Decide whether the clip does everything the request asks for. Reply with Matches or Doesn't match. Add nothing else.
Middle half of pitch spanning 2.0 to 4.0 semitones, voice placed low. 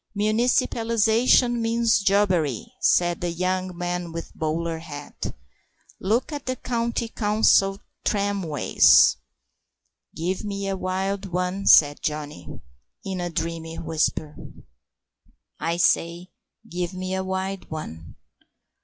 Doesn't match